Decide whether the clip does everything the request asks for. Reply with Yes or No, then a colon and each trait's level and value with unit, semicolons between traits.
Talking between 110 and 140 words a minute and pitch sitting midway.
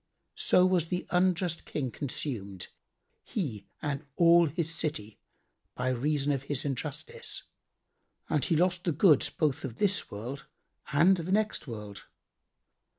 Yes: slow, 135 wpm; medium, 150 Hz